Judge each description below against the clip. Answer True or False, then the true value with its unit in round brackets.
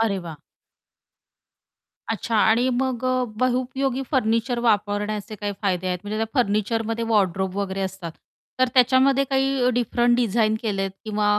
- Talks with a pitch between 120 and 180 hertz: False (225 Hz)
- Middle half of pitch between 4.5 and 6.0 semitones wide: False (3.5 semitones)